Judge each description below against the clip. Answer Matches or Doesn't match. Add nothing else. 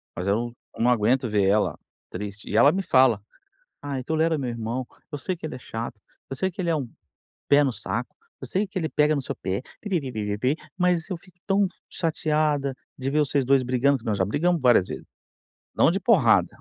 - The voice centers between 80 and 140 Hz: Matches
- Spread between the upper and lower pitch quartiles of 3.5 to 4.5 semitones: Doesn't match